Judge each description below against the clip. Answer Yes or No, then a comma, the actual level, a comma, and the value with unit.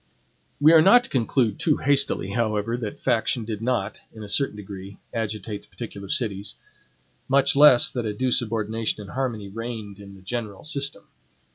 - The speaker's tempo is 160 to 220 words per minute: Yes, average, 170 wpm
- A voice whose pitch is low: Yes, low, 115 Hz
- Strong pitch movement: No, average, 3.8 semitones